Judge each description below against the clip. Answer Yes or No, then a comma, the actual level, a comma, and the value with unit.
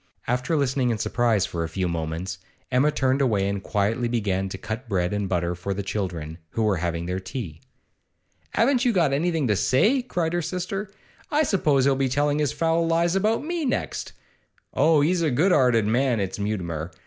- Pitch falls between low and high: No, low, 125 Hz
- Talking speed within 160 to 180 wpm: No, average, 195 wpm